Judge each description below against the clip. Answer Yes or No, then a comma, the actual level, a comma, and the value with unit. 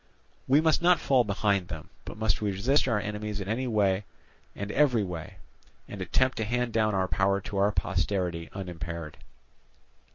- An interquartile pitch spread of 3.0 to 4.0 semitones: Yes, average, 3.6 semitones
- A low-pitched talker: Yes, low, 100 Hz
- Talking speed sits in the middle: Yes, average, 170 wpm